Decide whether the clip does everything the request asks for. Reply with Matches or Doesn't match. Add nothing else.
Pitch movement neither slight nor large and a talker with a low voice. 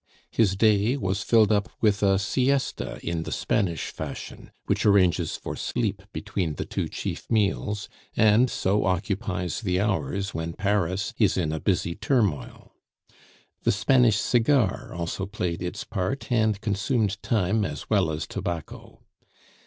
Matches